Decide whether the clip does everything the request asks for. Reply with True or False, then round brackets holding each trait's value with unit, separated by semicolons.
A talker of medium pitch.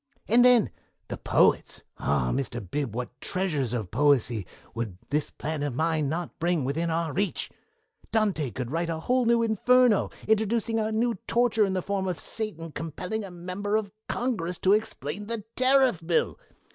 True (180 Hz)